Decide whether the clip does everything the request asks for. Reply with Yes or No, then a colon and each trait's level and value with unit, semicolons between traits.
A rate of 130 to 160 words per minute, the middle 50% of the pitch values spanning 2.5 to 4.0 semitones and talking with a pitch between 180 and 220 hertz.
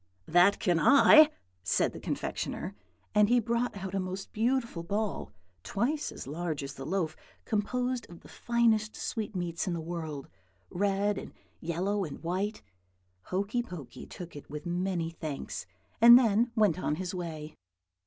No: average, 155 wpm; average, 4.6 semitones; high, 190 Hz